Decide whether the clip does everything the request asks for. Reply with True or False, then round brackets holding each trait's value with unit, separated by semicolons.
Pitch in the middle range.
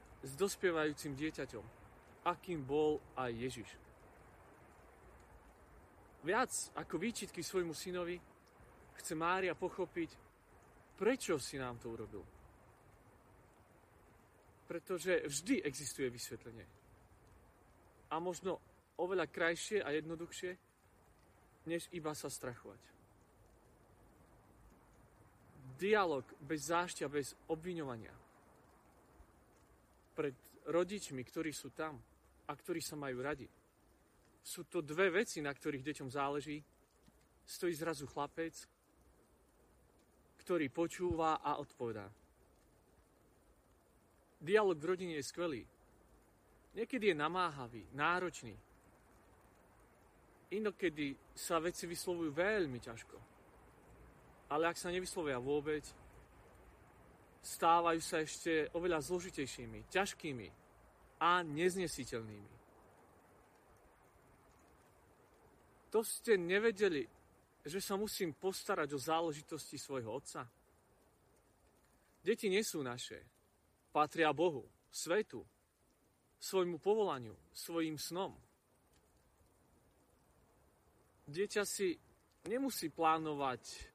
True (155 Hz)